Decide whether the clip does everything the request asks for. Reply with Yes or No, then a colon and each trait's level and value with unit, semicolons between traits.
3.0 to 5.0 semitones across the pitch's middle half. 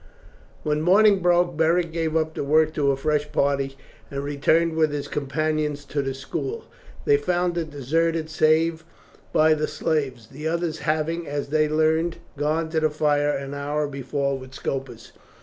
No: narrow, 2.4 semitones